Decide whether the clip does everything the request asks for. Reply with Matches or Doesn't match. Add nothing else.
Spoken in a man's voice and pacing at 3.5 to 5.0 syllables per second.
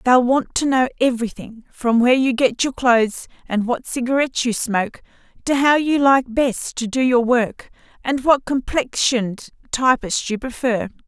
Doesn't match